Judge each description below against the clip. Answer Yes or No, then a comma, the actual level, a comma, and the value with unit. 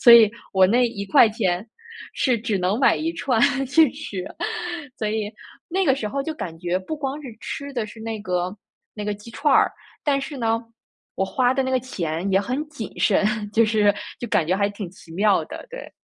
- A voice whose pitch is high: Yes, high, 220 Hz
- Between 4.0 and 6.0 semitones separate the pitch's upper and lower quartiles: Yes, average, 4.8 semitones